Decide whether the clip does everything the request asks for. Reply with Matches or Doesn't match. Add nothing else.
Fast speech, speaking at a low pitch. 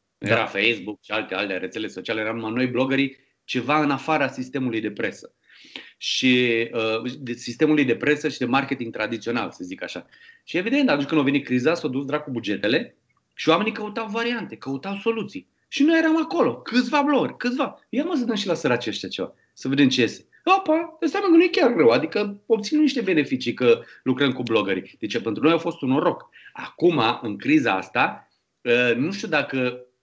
Doesn't match